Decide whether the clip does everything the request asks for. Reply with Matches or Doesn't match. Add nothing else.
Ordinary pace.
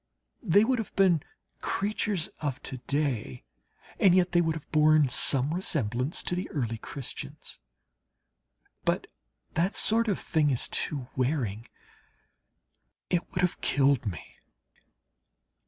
Doesn't match